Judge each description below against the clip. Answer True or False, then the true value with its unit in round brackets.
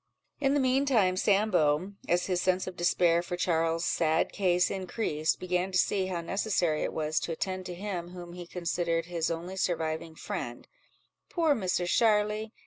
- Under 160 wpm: False (165 wpm)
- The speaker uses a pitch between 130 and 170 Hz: False (180 Hz)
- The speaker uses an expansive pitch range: False (2.6 semitones)